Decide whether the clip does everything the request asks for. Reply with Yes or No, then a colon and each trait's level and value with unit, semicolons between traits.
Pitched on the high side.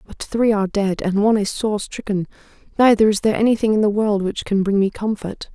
Yes: high, 210 Hz